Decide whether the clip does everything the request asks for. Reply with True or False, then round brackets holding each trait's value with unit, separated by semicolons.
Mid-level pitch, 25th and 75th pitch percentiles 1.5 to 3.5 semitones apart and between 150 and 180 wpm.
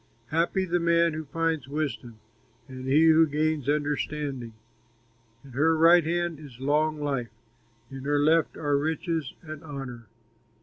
False (150 Hz; 2.7 semitones; 140 wpm)